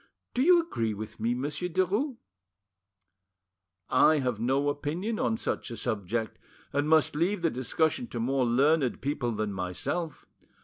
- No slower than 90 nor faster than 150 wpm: Yes, average, 145 wpm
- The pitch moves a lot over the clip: Yes, wide, 6.7 semitones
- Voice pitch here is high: No, medium, 145 Hz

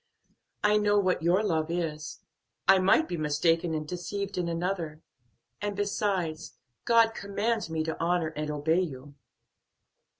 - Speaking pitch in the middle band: Yes, medium, 175 Hz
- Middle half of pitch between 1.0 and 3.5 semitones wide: No, average, 4.1 semitones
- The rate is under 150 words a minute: Yes, average, 140 wpm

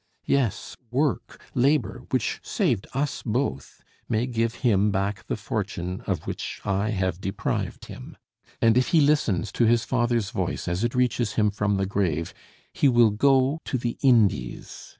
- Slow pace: No, average, 155 wpm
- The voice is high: No, low, 110 Hz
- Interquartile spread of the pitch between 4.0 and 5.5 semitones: Yes, average, 4.4 semitones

